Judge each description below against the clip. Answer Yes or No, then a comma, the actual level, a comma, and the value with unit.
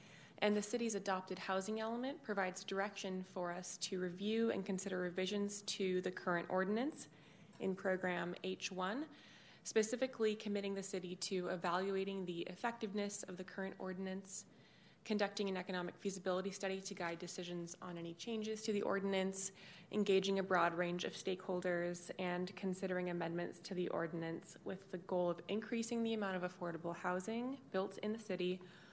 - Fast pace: No, average, 155 wpm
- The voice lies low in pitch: No, high, 190 Hz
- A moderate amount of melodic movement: No, narrow, 2.1 semitones